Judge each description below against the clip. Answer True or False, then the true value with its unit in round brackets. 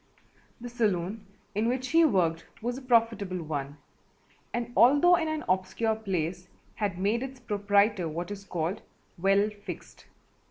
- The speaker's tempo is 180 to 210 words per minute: False (145 wpm)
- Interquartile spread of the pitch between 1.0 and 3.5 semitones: False (4.7 semitones)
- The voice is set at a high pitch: True (205 Hz)